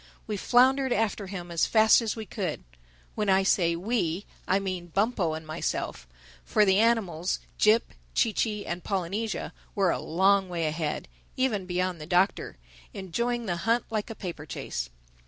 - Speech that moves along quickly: No, average, 155 wpm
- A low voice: No, high, 190 Hz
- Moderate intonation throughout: Yes, average, 4.2 semitones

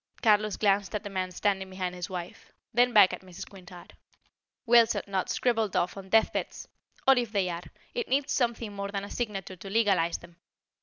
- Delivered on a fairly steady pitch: No, average, 3.2 semitones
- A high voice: Yes, high, 200 Hz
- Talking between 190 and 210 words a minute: Yes, average, 195 wpm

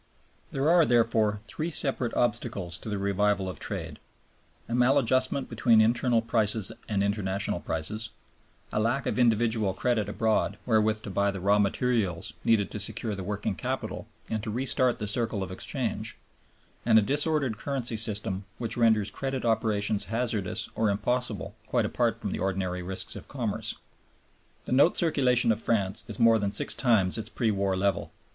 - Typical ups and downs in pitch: Yes, average, 3.2 semitones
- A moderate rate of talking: Yes, average, 165 wpm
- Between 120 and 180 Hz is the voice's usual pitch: No, low, 110 Hz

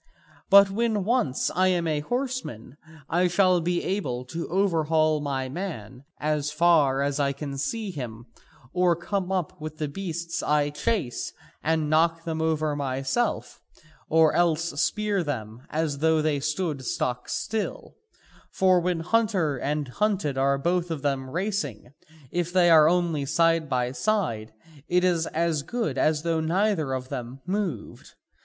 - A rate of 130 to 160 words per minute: Yes, average, 150 wpm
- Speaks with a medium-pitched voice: Yes, medium, 160 Hz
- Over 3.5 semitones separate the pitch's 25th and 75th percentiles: Yes, average, 4.4 semitones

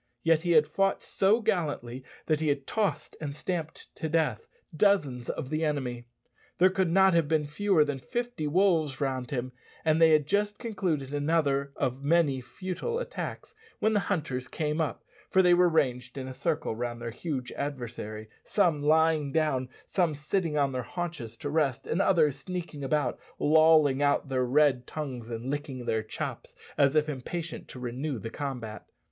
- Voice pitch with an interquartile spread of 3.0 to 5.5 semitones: Yes, average, 4.3 semitones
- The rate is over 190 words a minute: No, average, 175 wpm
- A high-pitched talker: No, medium, 150 Hz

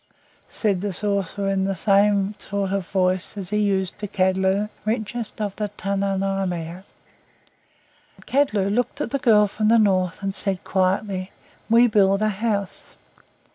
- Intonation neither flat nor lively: No, narrow, 1.7 semitones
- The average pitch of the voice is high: Yes, high, 195 Hz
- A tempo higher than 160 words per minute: No, average, 145 wpm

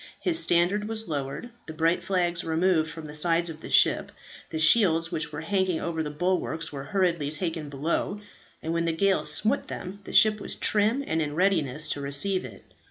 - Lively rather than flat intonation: No, average, 3.3 semitones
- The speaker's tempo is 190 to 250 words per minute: Yes, average, 195 wpm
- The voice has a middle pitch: Yes, medium, 165 Hz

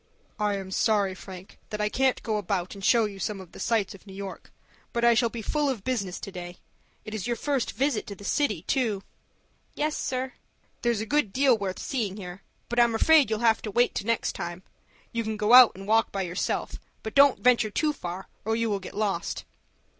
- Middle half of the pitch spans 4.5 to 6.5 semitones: No, average, 3.6 semitones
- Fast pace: Yes, fast, 220 wpm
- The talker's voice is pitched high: Yes, high, 215 Hz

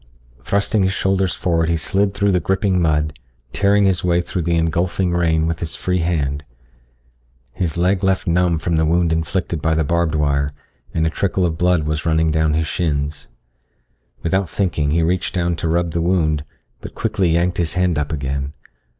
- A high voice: No, very low, 85 Hz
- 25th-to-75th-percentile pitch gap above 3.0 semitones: No, narrow, 2.4 semitones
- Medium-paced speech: Yes, average, 185 wpm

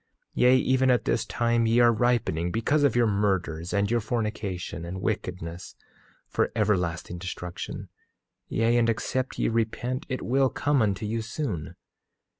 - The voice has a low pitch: Yes, low, 110 Hz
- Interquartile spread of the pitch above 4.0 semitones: Yes, average, 4.5 semitones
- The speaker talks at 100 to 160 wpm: Yes, average, 155 wpm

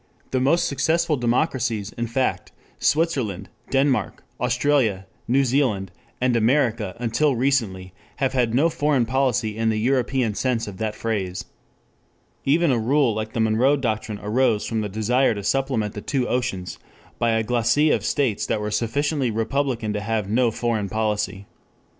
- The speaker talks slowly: No, average, 155 wpm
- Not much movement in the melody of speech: No, average, 3.8 semitones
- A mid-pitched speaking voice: No, low, 120 Hz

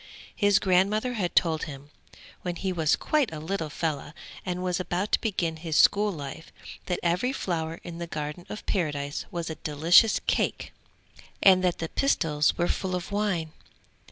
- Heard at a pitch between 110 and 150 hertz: No, medium, 175 Hz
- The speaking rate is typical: Yes, average, 170 wpm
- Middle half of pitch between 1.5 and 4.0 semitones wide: Yes, average, 3.4 semitones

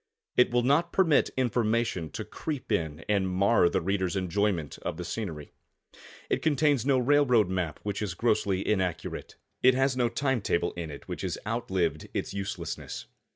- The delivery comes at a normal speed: Yes, average, 165 wpm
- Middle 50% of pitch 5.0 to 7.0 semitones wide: Yes, wide, 5.6 semitones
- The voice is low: Yes, low, 105 Hz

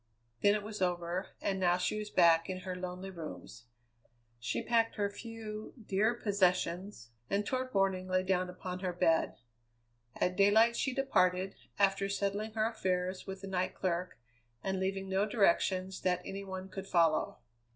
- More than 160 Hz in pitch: Yes, high, 190 Hz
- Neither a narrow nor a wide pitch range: No, narrow, 2.0 semitones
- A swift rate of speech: No, average, 160 wpm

